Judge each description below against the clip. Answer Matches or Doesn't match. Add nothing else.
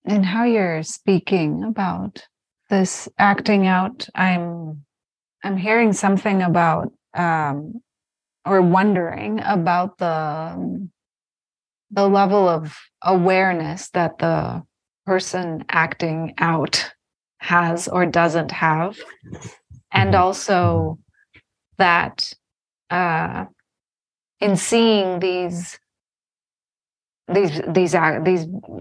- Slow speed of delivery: Matches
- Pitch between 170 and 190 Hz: Matches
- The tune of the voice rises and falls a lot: Doesn't match